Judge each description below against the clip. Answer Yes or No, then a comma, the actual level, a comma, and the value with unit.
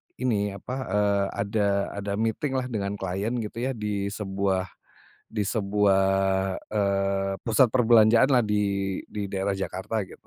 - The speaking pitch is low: Yes, low, 100 Hz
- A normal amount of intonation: No, narrow, 2.1 semitones